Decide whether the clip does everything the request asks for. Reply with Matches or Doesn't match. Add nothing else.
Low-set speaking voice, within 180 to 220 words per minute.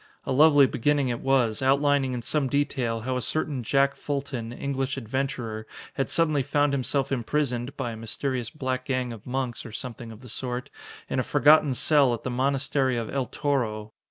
Matches